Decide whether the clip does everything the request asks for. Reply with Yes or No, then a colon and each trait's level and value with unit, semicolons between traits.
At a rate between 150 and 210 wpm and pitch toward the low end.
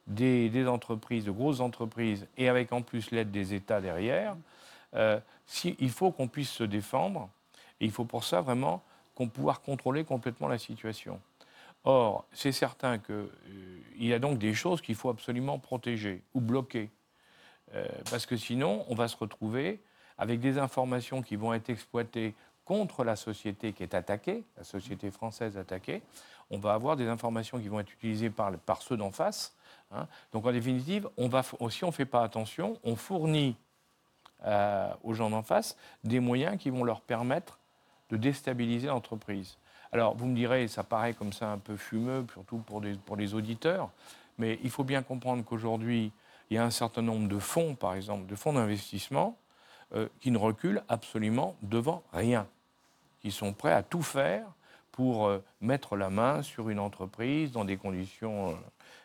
Yes: average, 180 wpm; low, 115 Hz